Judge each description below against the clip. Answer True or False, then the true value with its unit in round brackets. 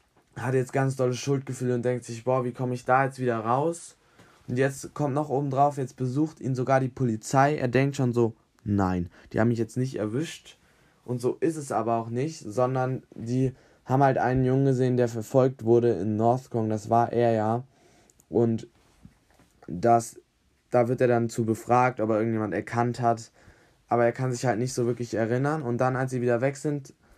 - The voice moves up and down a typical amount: False (2.1 semitones)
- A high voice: False (125 Hz)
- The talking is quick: True (200 wpm)